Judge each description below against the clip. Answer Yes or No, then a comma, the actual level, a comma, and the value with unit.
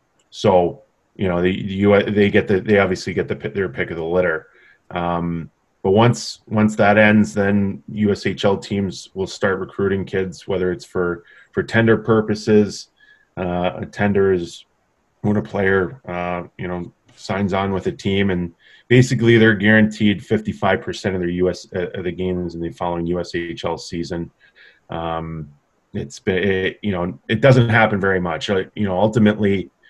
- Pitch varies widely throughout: No, average, 3.0 semitones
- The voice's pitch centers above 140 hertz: No, low, 100 Hz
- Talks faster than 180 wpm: No, average, 170 wpm